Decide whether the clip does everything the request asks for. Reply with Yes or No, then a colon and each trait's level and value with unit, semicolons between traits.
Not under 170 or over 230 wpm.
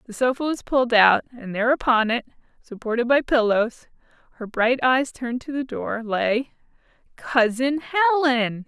No: average, 145 wpm